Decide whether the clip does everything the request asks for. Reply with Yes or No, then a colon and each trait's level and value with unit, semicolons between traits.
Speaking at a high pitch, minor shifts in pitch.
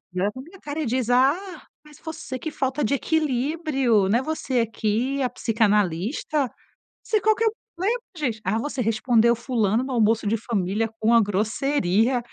No: high, 245 Hz; average, 4.8 semitones